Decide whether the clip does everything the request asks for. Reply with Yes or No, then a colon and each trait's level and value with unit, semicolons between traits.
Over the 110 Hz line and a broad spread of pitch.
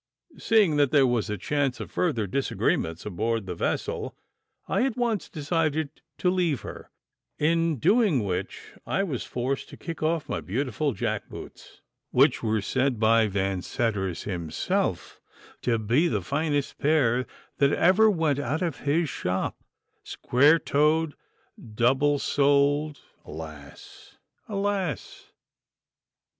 Yes: medium, 140 Hz; wide, 6.1 semitones